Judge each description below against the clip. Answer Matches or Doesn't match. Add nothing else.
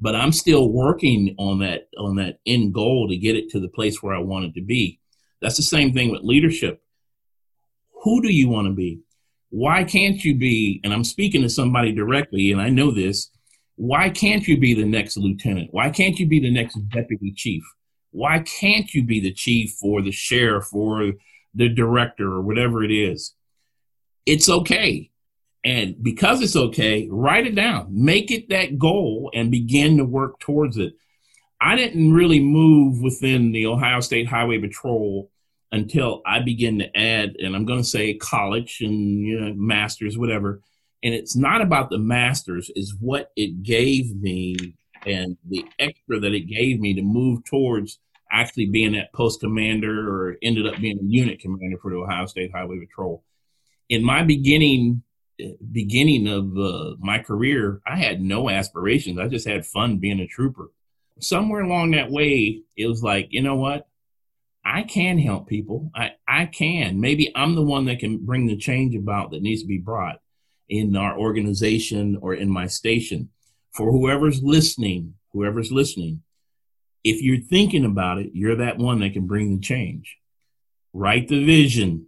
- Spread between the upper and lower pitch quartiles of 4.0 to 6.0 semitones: Matches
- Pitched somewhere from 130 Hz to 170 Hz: Doesn't match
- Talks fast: Doesn't match